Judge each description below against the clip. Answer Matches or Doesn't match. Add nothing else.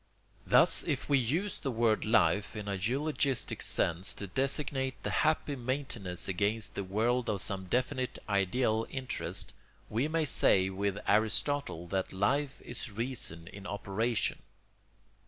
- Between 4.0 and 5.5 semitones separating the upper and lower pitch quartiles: Matches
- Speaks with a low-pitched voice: Matches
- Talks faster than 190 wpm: Doesn't match